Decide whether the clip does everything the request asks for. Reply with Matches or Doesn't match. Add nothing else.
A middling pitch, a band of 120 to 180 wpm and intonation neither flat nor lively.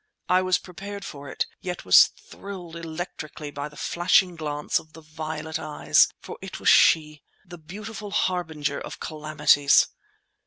Matches